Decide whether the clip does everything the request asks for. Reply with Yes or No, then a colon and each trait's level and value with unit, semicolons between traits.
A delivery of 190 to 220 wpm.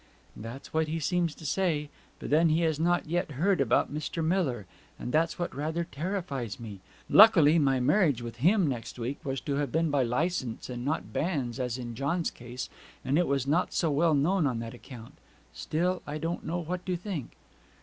Yes: average, 200 wpm